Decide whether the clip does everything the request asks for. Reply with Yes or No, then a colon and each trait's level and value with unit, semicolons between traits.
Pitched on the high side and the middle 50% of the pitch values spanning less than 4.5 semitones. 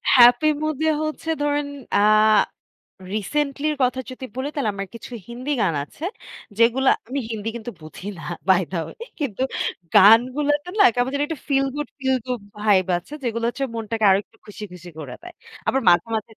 No: high, 245 Hz; average, 5.2 semitones